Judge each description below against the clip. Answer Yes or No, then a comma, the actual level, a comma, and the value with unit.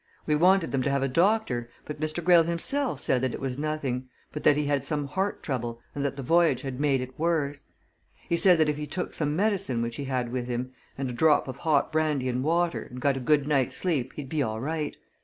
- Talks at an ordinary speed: No, fast, 245 wpm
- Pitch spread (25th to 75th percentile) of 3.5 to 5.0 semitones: Yes, average, 3.8 semitones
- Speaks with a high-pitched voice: No, medium, 145 Hz